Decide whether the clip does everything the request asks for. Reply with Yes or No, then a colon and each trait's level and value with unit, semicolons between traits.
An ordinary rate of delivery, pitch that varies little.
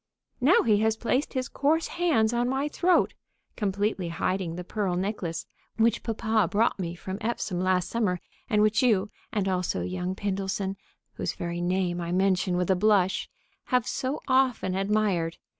No: average, 160 wpm; average, 3.9 semitones